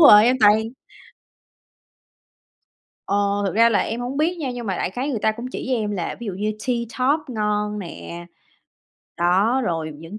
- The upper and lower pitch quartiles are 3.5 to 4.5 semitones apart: Yes, average, 4.1 semitones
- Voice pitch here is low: No, high, 215 Hz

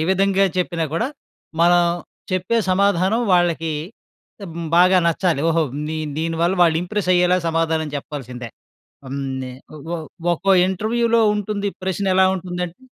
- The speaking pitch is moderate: Yes, medium, 180 Hz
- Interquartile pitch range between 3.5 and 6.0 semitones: No, average, 2.7 semitones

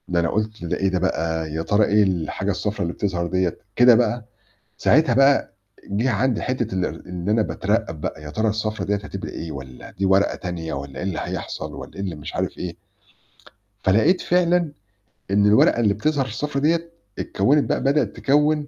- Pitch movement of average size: No, wide, 6.4 semitones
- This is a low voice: Yes, low, 105 Hz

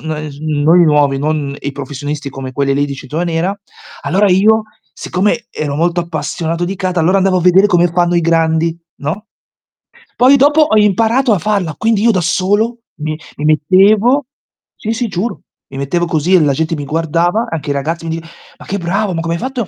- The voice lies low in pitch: No, medium, 175 Hz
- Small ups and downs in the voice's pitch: No, average, 4.8 semitones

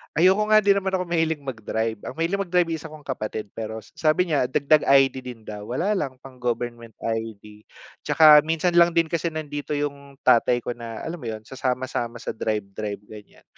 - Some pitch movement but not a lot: No, wide, 6.2 semitones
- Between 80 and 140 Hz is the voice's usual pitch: Yes, low, 135 Hz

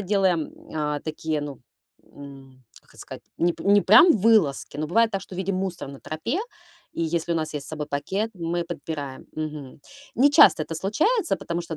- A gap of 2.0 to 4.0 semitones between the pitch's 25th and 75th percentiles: No, average, 4.6 semitones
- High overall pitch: No, medium, 165 Hz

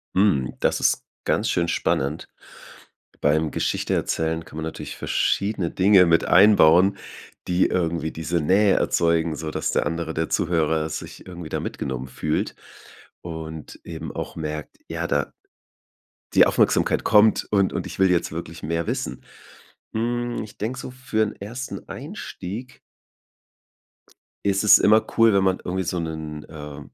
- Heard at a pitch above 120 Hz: No, very low, 85 Hz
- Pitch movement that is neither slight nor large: Yes, average, 4.2 semitones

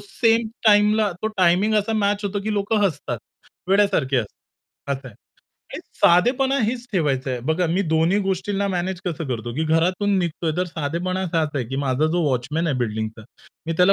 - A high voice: No, medium, 175 Hz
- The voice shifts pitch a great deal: Yes, wide, 6.0 semitones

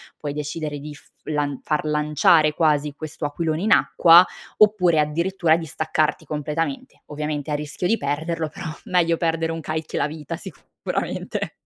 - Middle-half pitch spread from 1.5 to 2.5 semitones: Yes, narrow, 1.8 semitones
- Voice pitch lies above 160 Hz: No, medium, 155 Hz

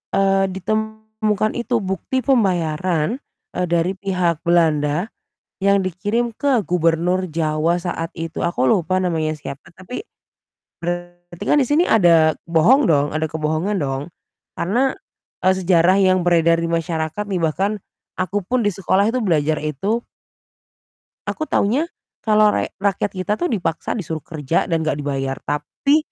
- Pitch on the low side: No, medium, 180 Hz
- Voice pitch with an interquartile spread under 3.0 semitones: No, average, 4.3 semitones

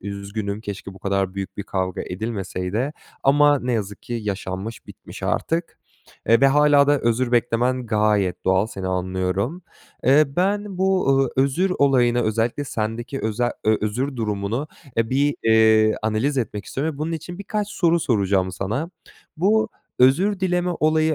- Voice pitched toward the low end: Yes, low, 120 Hz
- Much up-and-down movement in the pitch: Yes, wide, 6.2 semitones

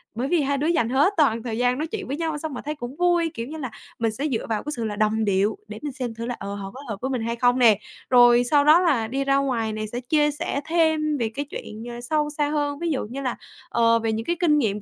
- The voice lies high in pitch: Yes, very high, 255 Hz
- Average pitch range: Yes, average, 4.7 semitones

